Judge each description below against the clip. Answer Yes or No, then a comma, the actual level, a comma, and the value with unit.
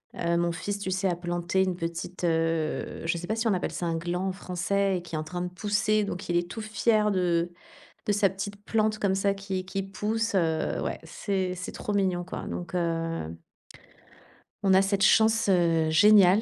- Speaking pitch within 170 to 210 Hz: Yes, medium, 185 Hz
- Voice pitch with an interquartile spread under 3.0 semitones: Yes, narrow, 2.6 semitones